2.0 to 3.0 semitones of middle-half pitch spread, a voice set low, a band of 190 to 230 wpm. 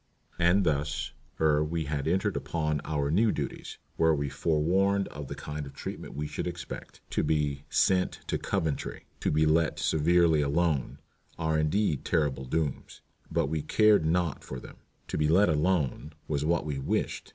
No: average, 2.7 semitones; very low, 80 Hz; average, 170 wpm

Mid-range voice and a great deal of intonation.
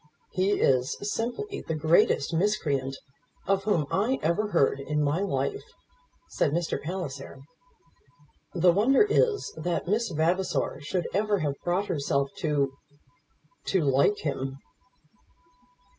Yes: medium, 175 Hz; wide, 6.0 semitones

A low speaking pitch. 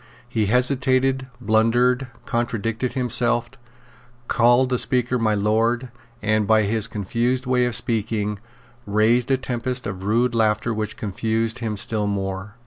Yes: low, 115 Hz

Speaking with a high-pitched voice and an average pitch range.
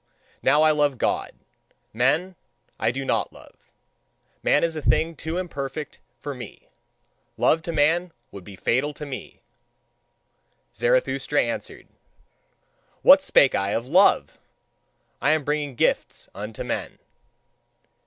No: medium, 150 Hz; average, 3.8 semitones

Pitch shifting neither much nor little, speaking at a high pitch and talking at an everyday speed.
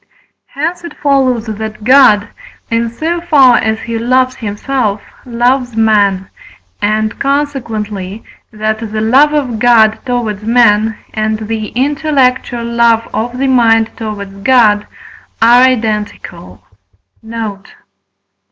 No: average, 3.0 semitones; high, 230 Hz; slow, 115 wpm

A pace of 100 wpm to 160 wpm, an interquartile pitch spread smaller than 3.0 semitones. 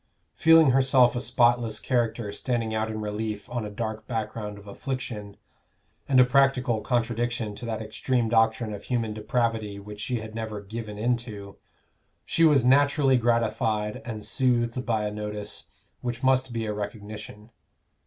Yes: average, 155 wpm; narrow, 2.6 semitones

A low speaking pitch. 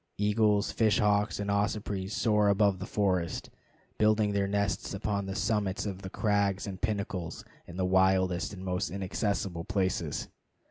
Yes: low, 100 Hz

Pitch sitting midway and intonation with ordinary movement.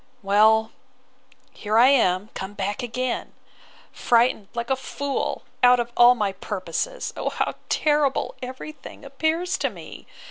No: high, 240 Hz; average, 4.5 semitones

